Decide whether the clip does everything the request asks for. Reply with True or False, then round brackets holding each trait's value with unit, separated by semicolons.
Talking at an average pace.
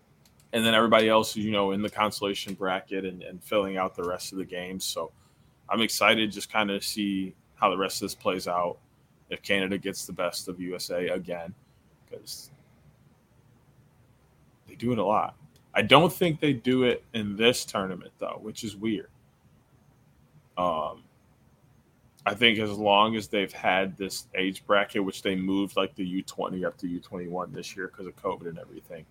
True (180 wpm)